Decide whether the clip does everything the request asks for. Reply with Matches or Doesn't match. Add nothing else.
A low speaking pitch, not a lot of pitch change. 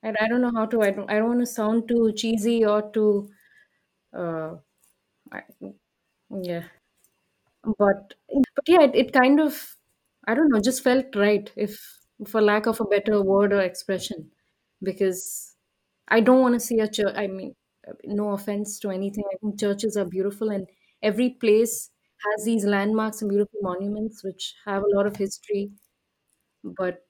Doesn't match